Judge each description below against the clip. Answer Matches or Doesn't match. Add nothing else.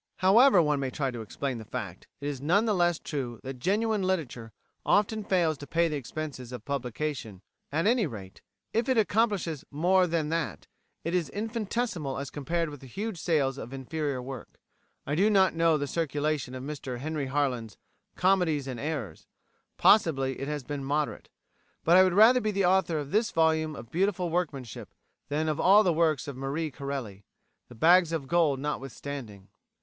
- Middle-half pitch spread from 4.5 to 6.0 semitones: Matches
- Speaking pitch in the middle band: Matches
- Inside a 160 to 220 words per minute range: Matches